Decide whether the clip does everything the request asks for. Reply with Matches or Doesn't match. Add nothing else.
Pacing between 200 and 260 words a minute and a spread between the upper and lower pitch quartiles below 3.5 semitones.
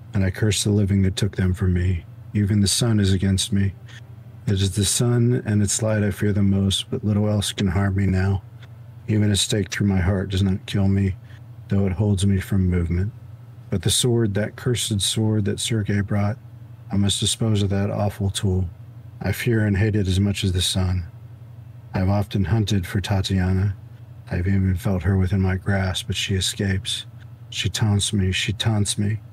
Matches